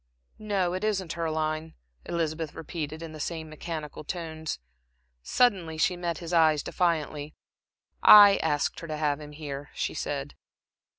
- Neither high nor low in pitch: Yes, medium, 160 Hz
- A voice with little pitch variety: Yes, narrow, 2.1 semitones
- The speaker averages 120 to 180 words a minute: Yes, average, 150 wpm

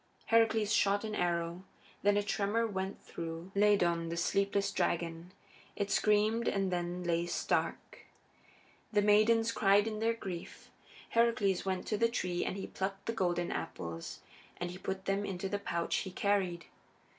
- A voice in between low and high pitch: No, high, 195 Hz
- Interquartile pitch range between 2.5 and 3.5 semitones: Yes, average, 3.0 semitones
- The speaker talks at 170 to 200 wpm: No, average, 155 wpm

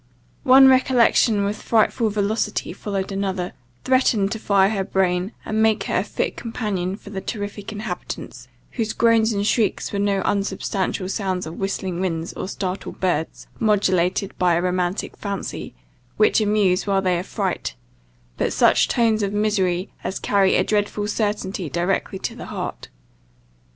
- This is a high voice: Yes, high, 200 Hz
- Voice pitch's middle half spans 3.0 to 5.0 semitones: No, narrow, 2.5 semitones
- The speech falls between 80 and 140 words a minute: No, average, 150 wpm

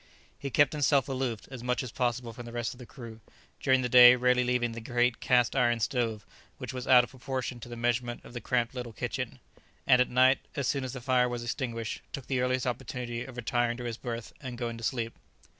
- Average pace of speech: No, fast, 230 wpm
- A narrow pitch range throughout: Yes, narrow, 1.3 semitones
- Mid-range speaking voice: No, low, 125 Hz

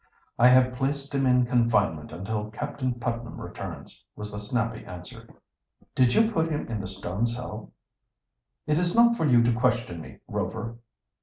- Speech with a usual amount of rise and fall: Yes, average, 3.8 semitones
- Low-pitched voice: Yes, low, 120 Hz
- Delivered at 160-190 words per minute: Yes, average, 165 wpm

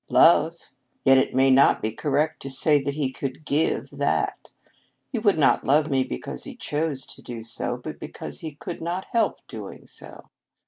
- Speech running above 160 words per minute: Yes, average, 185 wpm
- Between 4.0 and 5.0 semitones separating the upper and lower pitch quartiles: No, average, 3.2 semitones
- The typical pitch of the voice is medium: Yes, medium, 145 Hz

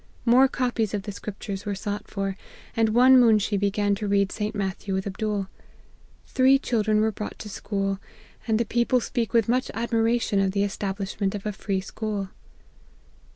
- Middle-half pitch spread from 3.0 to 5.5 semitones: No, narrow, 2.4 semitones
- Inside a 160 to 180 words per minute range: Yes, average, 170 wpm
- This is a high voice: Yes, high, 210 Hz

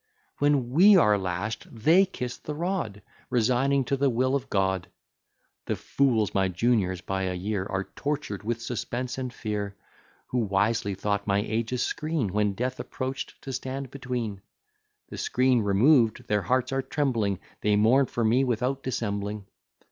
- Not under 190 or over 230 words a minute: No, average, 160 wpm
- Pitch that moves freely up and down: No, average, 4.4 semitones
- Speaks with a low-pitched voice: Yes, low, 115 Hz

